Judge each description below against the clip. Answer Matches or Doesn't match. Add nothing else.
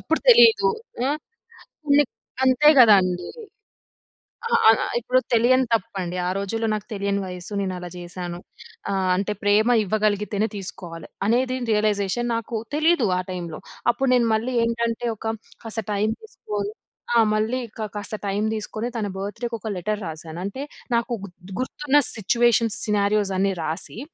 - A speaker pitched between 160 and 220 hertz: Matches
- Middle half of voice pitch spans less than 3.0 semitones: Doesn't match